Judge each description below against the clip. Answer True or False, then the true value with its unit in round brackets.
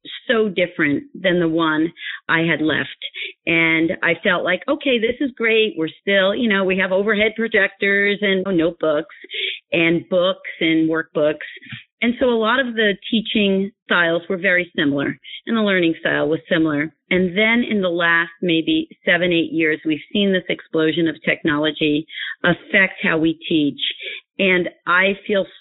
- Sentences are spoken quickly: False (165 wpm)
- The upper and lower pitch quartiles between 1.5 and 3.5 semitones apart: False (5.0 semitones)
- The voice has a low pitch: False (190 Hz)